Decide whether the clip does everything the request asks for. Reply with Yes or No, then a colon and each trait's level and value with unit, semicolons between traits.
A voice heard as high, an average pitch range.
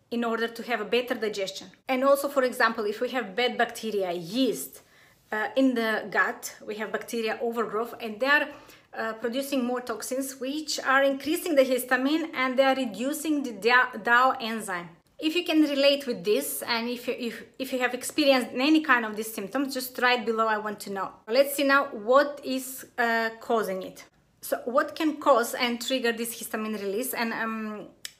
Yes: high, 245 Hz; average, 3.1 semitones